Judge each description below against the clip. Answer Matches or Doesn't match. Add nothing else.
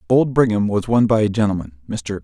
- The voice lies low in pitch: Matches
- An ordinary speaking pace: Matches